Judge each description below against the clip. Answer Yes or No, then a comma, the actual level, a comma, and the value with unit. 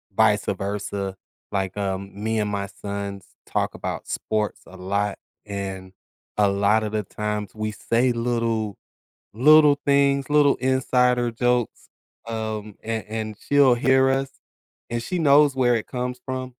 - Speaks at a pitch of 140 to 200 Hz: No, low, 110 Hz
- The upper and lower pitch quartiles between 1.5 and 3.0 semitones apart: No, average, 3.9 semitones